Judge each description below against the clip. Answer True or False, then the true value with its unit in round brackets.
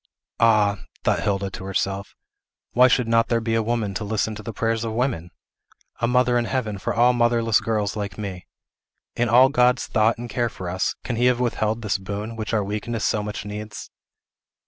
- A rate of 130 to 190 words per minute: False (200 wpm)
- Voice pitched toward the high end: False (110 Hz)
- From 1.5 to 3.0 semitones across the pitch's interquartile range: True (2.4 semitones)